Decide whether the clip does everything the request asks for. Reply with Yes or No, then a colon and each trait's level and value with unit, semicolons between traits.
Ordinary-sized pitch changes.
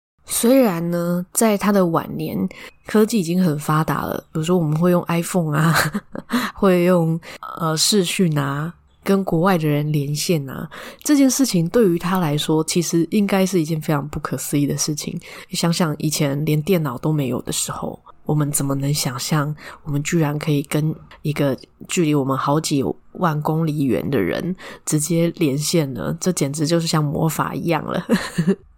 Yes: average, 3.5 semitones